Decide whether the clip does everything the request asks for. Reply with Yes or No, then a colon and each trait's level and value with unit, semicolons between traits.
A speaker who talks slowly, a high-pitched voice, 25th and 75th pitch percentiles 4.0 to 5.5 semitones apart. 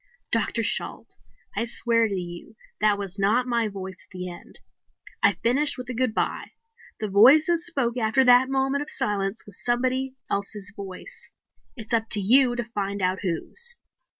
No: average, 170 wpm; high, 225 Hz; average, 4.4 semitones